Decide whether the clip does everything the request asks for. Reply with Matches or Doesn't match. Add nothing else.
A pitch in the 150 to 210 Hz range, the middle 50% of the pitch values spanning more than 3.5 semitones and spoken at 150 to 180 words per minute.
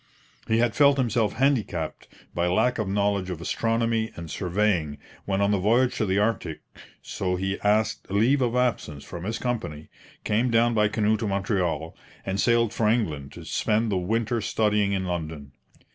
Doesn't match